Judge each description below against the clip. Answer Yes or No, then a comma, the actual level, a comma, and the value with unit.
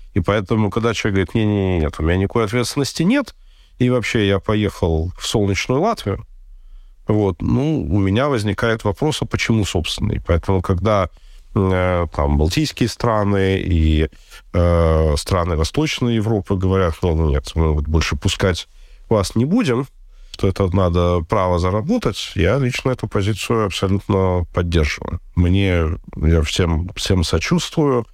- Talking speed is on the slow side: No, average, 145 wpm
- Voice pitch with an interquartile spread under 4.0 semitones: No, average, 4.3 semitones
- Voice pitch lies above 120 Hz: No, very low, 95 Hz